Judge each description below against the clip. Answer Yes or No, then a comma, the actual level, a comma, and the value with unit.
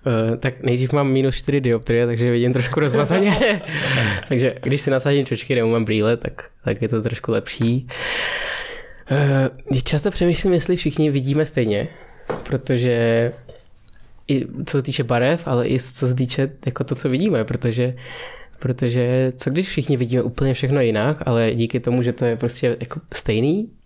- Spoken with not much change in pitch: No, average, 3.0 semitones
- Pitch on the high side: No, low, 130 Hz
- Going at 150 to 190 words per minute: Yes, average, 165 wpm